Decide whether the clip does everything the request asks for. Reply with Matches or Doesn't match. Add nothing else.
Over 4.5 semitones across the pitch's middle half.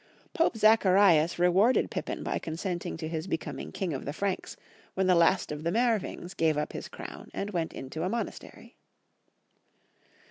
Doesn't match